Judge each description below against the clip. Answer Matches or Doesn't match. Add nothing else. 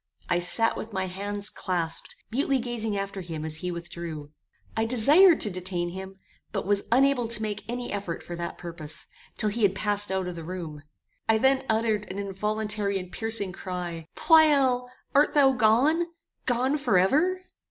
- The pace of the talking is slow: Doesn't match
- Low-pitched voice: Doesn't match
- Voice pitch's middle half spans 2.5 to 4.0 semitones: Doesn't match